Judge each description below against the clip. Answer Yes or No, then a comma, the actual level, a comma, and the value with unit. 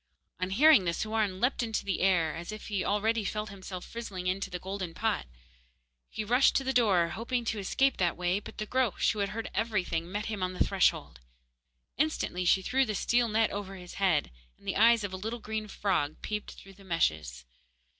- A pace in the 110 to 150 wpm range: No, fast, 205 wpm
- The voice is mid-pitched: No, high, 200 Hz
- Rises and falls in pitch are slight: No, average, 3.4 semitones